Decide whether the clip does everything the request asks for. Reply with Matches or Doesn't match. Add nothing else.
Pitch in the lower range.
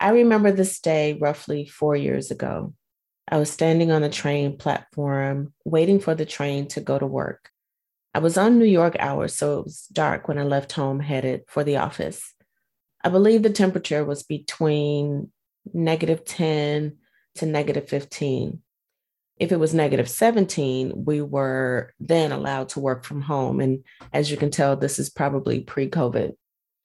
Doesn't match